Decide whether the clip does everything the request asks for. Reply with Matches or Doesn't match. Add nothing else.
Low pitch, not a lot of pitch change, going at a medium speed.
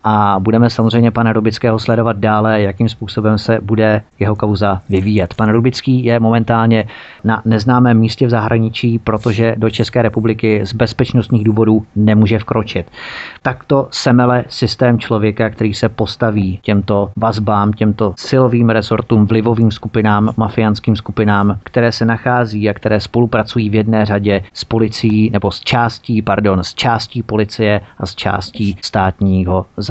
Matches